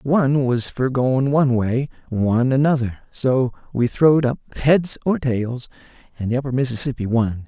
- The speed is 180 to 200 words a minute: No, average, 160 wpm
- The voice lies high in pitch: No, low, 130 Hz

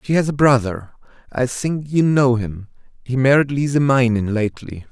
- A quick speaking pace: No, average, 170 wpm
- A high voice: No, low, 130 Hz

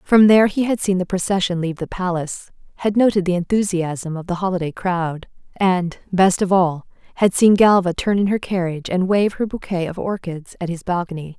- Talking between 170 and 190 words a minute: No, average, 200 wpm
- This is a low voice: No, medium, 185 Hz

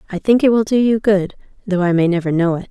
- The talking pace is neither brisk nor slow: No, fast, 290 wpm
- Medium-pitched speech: No, high, 195 Hz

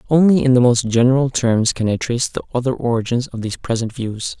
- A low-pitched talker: Yes, low, 120 Hz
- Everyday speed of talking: No, fast, 220 wpm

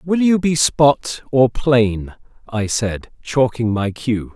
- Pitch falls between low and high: No, low, 125 Hz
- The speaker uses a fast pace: No, average, 150 wpm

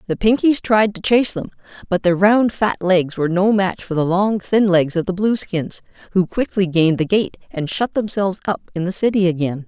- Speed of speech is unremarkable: No, fast, 215 wpm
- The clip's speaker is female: Yes, female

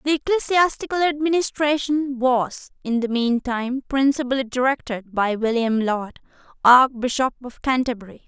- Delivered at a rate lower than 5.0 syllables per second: Yes, 4.8 syllables/s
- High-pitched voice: Yes, very high, 255 Hz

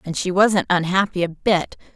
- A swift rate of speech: No, average, 185 wpm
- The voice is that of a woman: Yes, female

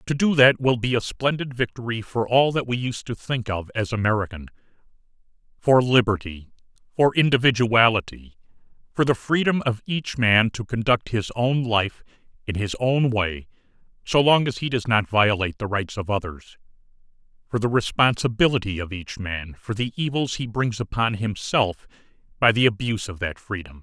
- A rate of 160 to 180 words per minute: Yes, average, 165 wpm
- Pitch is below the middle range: Yes, low, 115 Hz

